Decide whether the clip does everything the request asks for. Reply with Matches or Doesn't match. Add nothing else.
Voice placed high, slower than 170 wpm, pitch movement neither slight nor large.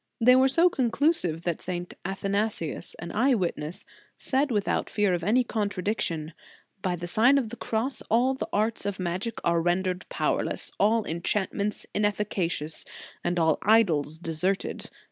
Matches